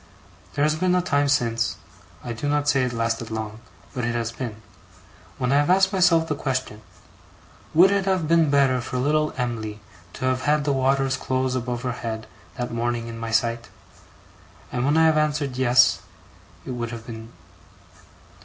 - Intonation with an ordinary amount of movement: Yes, average, 4.0 semitones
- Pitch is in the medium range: No, low, 130 Hz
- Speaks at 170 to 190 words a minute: Yes, average, 180 wpm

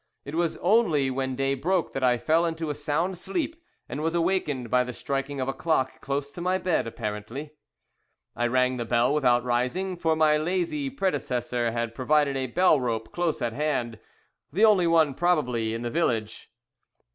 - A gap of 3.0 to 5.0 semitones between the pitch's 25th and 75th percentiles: No, wide, 5.4 semitones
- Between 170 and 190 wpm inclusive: Yes, average, 180 wpm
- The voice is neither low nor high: Yes, medium, 145 Hz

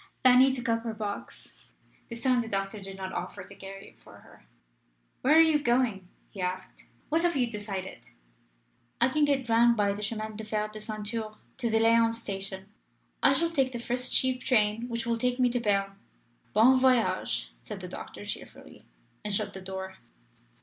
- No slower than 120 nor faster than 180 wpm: No, average, 190 wpm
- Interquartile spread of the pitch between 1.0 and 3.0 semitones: No, average, 3.7 semitones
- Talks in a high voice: Yes, high, 225 Hz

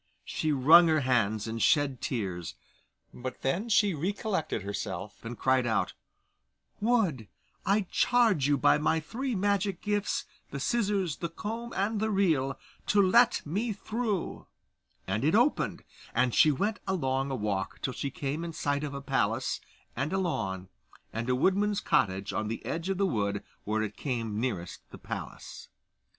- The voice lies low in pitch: No, medium, 150 Hz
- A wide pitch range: Yes, wide, 8.8 semitones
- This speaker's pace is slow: No, average, 165 wpm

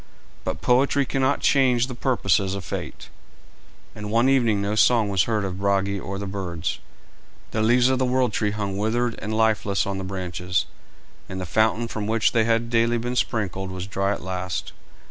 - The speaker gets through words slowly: No, average, 185 wpm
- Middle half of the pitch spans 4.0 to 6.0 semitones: No, average, 3.4 semitones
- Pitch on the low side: Yes, low, 105 Hz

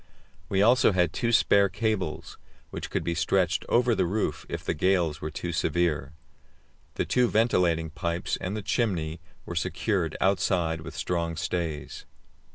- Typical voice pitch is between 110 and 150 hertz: No, very low, 90 Hz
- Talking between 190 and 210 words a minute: No, average, 155 wpm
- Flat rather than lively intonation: No, average, 3.5 semitones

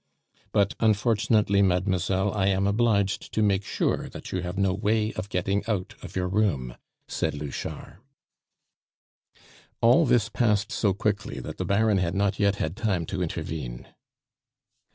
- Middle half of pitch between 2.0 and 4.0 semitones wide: Yes, narrow, 2.6 semitones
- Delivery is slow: No, average, 150 wpm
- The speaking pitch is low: Yes, low, 100 Hz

